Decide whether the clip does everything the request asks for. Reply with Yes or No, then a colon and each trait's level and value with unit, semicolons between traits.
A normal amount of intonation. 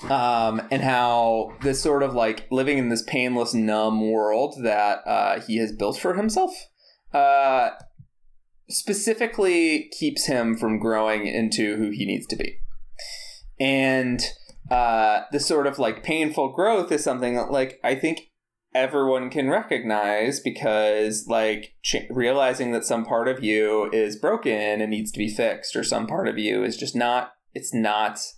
Yes: average, 4.2 semitones